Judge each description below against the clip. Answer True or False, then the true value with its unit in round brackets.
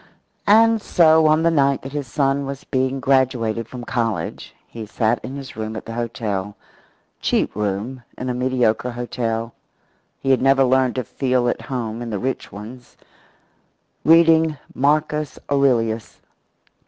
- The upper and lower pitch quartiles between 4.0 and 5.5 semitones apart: False (3.3 semitones)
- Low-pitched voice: True (130 Hz)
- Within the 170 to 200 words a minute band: False (150 wpm)